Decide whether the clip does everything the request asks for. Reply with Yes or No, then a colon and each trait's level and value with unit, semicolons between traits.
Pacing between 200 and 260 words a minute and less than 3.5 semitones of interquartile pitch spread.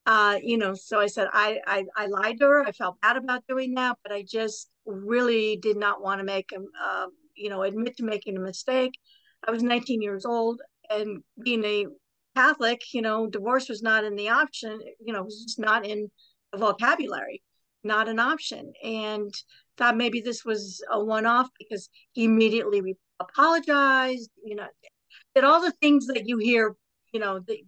No: average, 190 wpm; average, 2.8 semitones